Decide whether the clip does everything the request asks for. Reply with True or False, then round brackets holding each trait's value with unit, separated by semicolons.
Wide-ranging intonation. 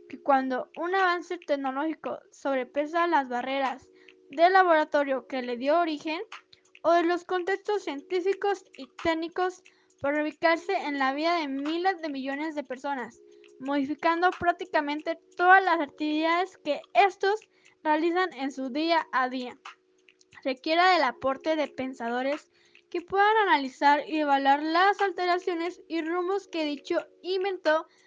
False (4.5 semitones)